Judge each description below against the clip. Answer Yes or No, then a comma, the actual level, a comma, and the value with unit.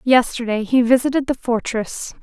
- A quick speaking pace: No, slow, 135 wpm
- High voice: Yes, high, 245 Hz